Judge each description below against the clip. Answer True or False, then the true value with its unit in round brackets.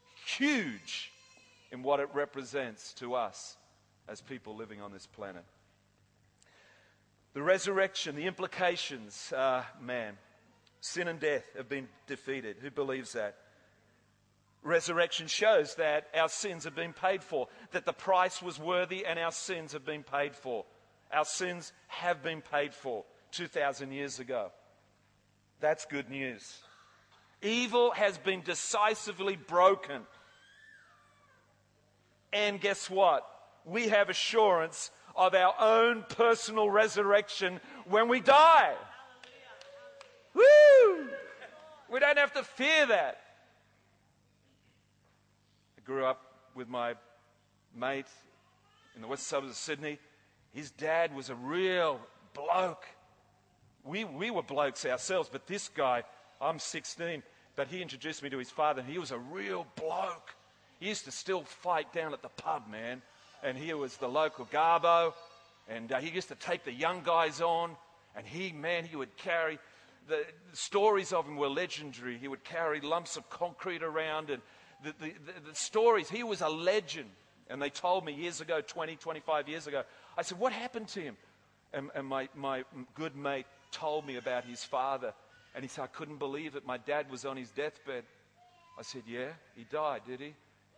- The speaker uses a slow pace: False (155 wpm)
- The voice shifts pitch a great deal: True (6.5 semitones)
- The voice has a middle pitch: True (155 Hz)